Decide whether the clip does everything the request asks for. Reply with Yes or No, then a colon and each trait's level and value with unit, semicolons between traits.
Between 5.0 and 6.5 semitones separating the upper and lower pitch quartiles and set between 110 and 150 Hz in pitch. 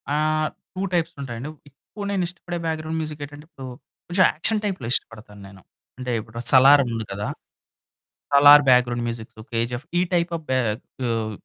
Yes: wide, 5.5 semitones; medium, 140 Hz